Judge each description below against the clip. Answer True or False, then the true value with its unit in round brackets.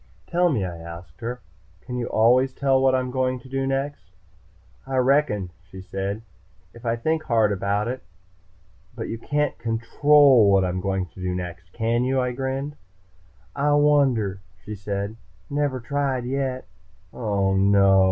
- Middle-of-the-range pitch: False (120 Hz)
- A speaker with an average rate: True (160 wpm)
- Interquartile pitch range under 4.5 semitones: False (5.4 semitones)